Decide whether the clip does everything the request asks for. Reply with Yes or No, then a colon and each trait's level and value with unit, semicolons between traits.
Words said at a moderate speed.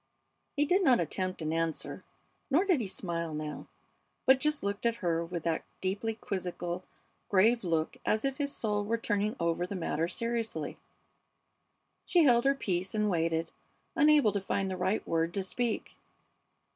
Yes: average, 165 wpm